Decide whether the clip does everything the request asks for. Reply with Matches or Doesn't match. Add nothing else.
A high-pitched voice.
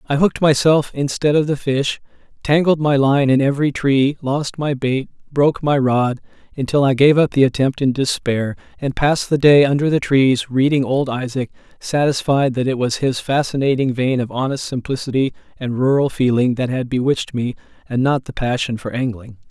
Doesn't match